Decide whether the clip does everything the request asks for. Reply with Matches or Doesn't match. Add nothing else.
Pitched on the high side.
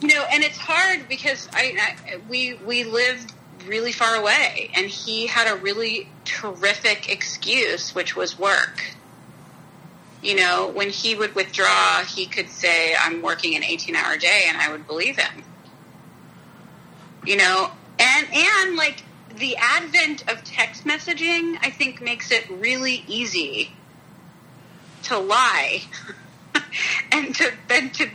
Matches